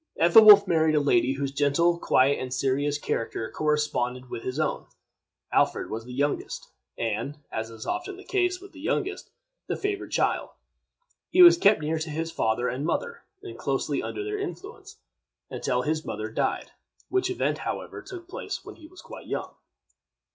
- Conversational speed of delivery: Yes, average, 170 wpm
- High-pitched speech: No, medium, 155 Hz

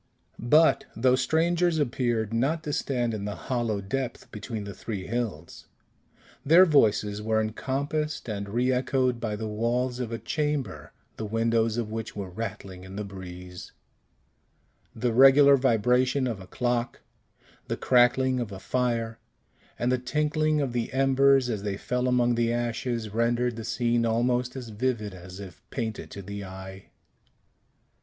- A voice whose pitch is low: Yes, low, 120 Hz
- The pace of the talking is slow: No, average, 150 wpm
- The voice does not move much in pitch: No, average, 3.4 semitones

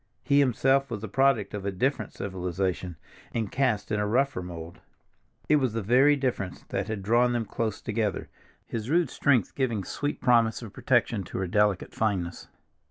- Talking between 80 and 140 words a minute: No, average, 175 wpm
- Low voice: Yes, low, 110 Hz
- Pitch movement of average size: Yes, average, 4.8 semitones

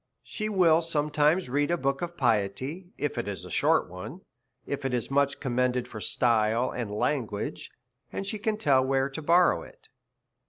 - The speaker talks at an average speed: Yes, average, 185 wpm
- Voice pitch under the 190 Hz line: Yes, medium, 140 Hz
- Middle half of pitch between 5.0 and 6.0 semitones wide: Yes, wide, 5.5 semitones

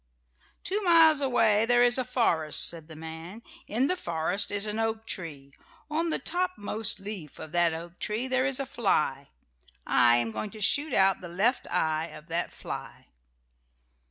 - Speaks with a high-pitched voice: Yes, high, 205 Hz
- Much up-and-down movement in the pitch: Yes, wide, 7.4 semitones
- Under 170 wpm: No, average, 180 wpm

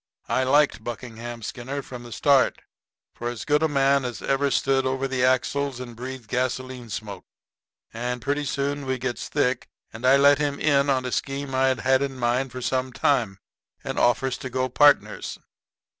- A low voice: Yes, low, 130 Hz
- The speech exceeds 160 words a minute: Yes, average, 180 wpm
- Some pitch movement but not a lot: No, narrow, 2.2 semitones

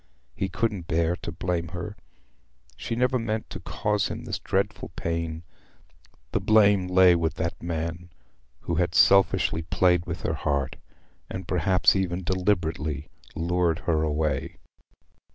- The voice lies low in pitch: Yes, very low, 85 Hz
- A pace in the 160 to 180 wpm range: No, slow, 135 wpm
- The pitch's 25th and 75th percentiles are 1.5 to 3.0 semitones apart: Yes, narrow, 2.5 semitones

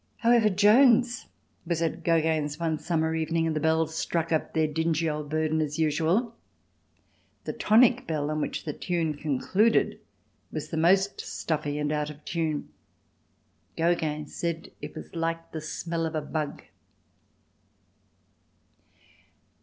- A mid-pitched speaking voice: Yes, medium, 160 Hz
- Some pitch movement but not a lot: No, narrow, 1.9 semitones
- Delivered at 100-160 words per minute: Yes, average, 140 wpm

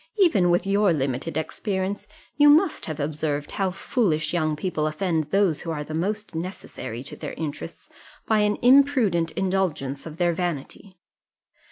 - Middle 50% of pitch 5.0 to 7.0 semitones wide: No, average, 4.6 semitones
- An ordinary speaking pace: Yes, average, 155 wpm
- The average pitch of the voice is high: No, medium, 175 Hz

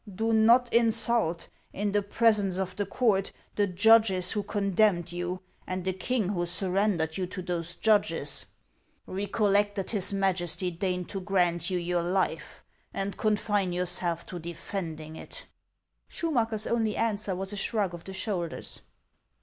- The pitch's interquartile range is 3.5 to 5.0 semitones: No, average, 3.0 semitones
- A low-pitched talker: No, high, 195 Hz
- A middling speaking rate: Yes, average, 150 wpm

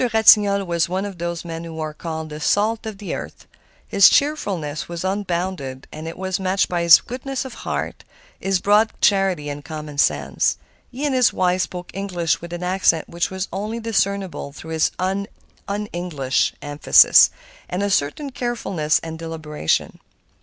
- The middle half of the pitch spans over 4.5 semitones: No, average, 3.8 semitones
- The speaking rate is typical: Yes, average, 165 wpm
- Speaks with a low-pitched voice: No, medium, 180 Hz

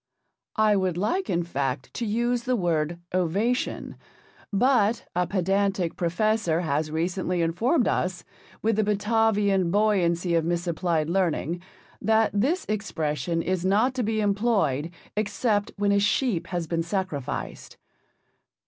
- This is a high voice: Yes, high, 195 Hz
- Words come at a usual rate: No, slow, 130 wpm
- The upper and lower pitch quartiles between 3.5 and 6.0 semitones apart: Yes, average, 4.2 semitones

